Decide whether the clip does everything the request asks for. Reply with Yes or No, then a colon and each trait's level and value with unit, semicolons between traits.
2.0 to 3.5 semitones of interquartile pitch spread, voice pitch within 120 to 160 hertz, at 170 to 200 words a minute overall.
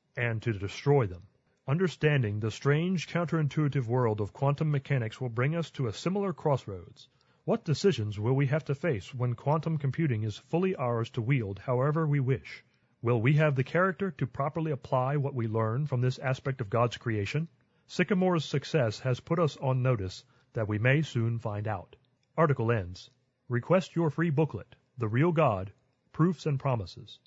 No: average, 4.5 semitones; low, 135 Hz; average, 175 wpm